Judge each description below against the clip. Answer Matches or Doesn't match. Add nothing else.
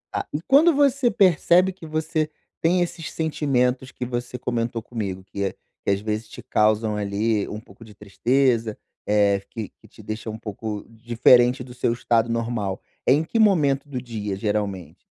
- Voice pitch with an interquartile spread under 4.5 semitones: Doesn't match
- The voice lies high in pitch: Doesn't match